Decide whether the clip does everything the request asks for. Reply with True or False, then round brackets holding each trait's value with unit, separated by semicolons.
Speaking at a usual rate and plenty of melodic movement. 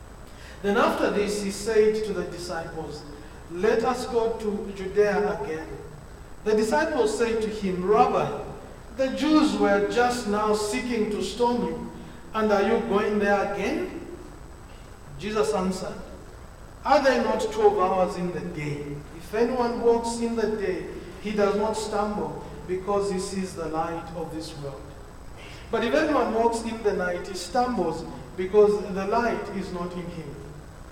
False (155 wpm; 4.1 semitones)